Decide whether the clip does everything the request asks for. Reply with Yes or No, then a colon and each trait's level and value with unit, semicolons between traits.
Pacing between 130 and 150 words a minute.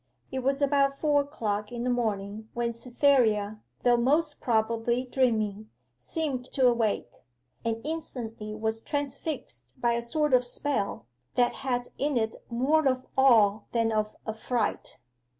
Yes: average, 140 wpm